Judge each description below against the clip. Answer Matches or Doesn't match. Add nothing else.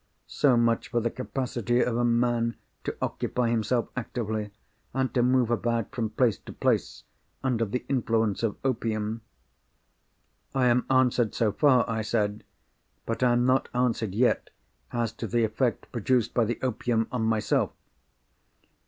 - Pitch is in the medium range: Doesn't match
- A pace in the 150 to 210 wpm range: Matches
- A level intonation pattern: Matches